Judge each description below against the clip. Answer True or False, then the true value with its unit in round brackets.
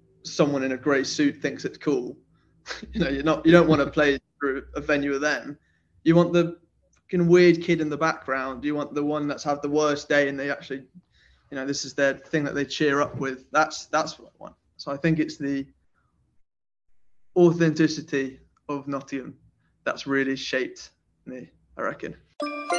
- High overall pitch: False (145 Hz)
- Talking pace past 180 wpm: True (190 wpm)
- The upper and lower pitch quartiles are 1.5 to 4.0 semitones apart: True (2.8 semitones)